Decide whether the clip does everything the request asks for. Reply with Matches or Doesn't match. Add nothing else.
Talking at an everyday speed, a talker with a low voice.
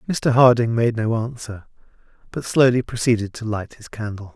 Matches